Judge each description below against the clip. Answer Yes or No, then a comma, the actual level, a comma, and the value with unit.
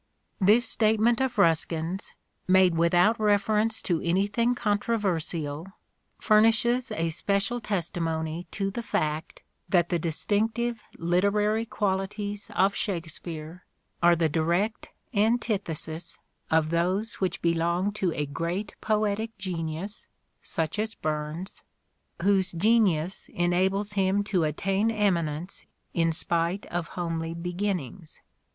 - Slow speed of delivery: Yes, slow, 110 wpm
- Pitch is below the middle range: No, high, 190 Hz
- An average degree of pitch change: Yes, average, 3.9 semitones